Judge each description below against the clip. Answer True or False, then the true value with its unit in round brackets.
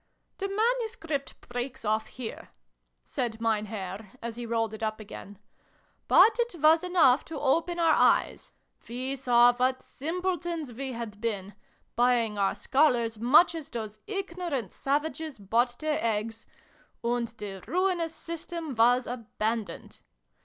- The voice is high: True (245 Hz)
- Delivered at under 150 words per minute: True (140 wpm)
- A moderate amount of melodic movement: False (6.2 semitones)